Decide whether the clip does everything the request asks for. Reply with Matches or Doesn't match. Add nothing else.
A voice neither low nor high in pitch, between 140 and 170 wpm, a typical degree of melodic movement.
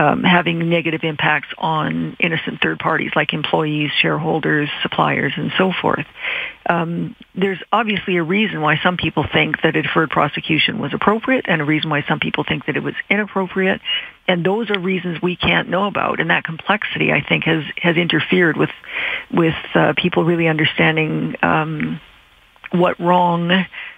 Matches